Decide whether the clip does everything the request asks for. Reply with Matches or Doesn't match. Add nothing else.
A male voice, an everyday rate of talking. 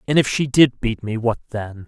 Doesn't match